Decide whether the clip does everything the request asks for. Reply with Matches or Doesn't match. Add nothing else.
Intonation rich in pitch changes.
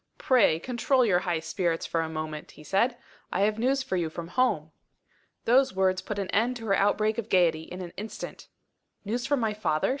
Matches